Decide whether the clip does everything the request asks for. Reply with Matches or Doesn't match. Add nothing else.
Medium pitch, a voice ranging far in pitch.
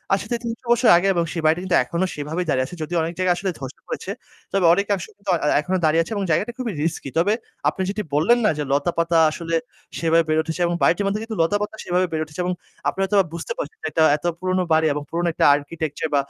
Doesn't match